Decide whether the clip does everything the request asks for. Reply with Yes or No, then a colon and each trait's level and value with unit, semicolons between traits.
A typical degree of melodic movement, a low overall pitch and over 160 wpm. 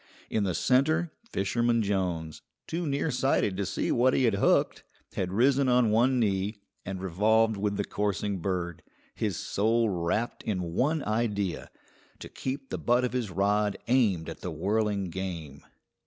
No: average, 4.4 semitones; low, 105 Hz; average, 155 wpm